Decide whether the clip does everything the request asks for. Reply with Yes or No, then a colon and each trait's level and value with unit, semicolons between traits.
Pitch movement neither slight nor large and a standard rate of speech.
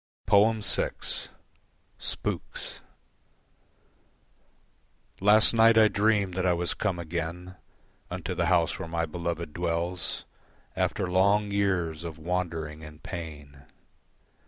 No: average, 3.3 semitones; slow, 105 wpm